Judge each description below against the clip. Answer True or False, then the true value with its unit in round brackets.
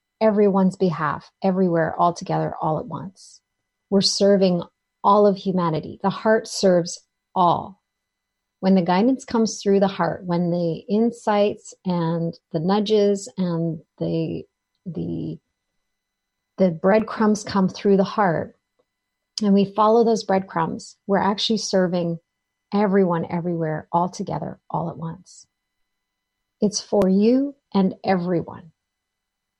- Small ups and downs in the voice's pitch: False (4.1 semitones)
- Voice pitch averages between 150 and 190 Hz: True (185 Hz)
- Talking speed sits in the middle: False (120 wpm)